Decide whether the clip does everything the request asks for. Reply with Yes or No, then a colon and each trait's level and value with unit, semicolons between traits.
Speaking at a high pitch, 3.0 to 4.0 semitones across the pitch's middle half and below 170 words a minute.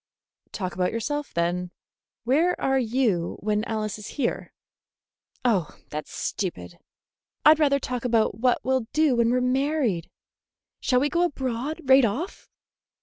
No: high, 245 Hz; average, 4.8 semitones; average, 145 wpm